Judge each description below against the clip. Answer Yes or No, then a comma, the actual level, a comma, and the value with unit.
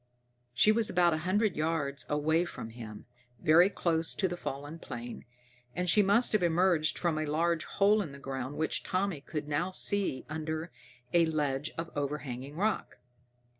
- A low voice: No, medium, 160 Hz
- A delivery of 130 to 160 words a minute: No, average, 170 wpm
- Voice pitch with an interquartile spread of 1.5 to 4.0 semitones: Yes, average, 3.6 semitones